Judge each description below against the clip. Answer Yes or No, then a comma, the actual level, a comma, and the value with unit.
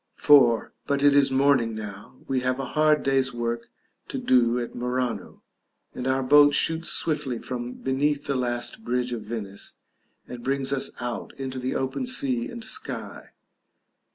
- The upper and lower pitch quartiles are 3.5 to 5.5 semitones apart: No, average, 2.7 semitones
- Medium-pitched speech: No, low, 130 Hz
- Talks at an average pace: Yes, average, 165 wpm